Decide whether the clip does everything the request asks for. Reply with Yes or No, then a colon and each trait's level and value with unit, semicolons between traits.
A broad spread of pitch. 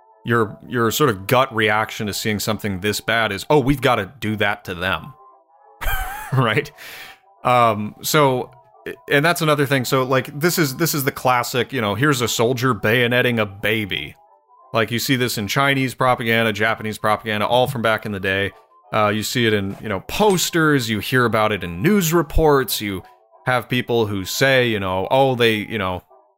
No: average, 3.8 semitones